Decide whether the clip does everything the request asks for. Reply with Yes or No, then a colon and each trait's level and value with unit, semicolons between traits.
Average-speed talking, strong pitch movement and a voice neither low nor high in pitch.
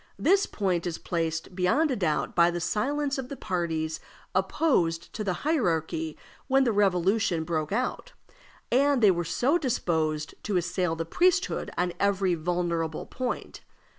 Yes: average, 150 wpm; wide, 7.3 semitones; medium, 180 Hz